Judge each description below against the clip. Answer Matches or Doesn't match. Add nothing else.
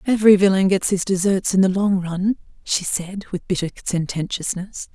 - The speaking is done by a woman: Matches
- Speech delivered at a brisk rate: Doesn't match